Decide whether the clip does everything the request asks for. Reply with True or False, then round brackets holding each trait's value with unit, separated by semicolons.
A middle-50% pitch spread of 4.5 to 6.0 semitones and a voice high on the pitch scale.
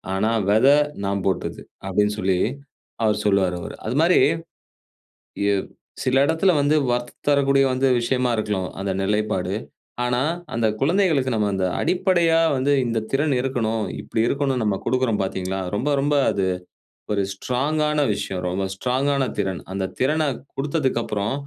False (5.6 semitones; 125 Hz)